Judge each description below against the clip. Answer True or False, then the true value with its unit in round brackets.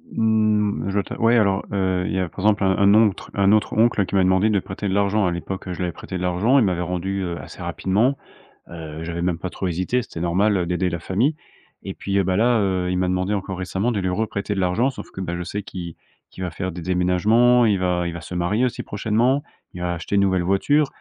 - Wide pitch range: False (2.8 semitones)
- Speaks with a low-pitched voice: True (95 Hz)